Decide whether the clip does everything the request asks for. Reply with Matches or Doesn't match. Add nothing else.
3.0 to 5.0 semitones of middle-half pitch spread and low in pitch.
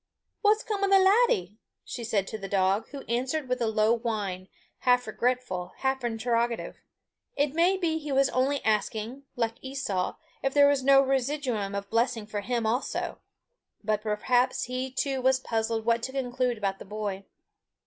Doesn't match